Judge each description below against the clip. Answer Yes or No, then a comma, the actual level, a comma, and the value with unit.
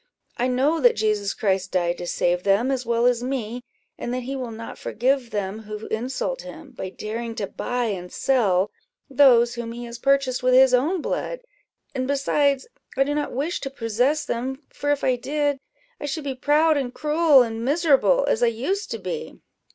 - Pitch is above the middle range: Yes, very high, 250 Hz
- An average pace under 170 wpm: No, average, 195 wpm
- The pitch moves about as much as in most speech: Yes, average, 3.7 semitones